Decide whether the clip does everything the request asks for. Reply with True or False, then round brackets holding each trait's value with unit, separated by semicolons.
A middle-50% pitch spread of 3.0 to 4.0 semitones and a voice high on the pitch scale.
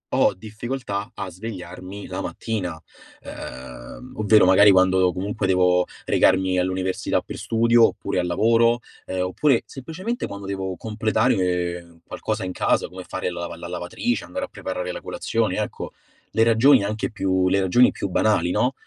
False (3.6 semitones; 95 Hz)